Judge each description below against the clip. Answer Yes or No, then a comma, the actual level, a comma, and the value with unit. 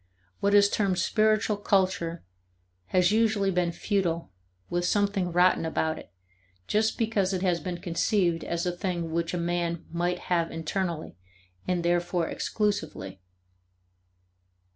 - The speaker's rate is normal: No, slow, 130 wpm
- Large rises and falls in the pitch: No, average, 2.8 semitones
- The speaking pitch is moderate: Yes, medium, 180 Hz